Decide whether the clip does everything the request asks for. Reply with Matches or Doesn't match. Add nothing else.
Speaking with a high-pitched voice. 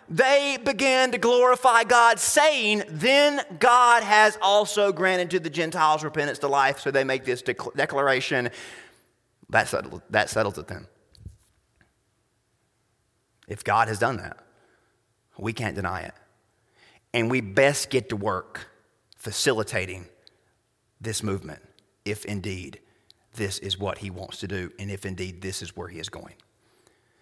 Doesn't match